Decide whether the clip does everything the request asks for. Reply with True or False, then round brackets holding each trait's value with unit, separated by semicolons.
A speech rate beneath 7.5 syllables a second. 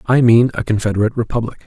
False (7.6 syllables/s)